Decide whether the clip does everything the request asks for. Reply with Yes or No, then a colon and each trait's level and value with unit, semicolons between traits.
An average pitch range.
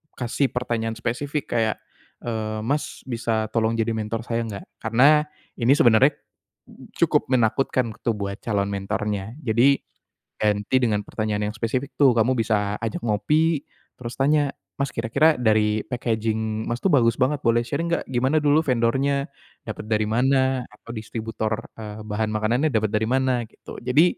Yes: average, 3.3 semitones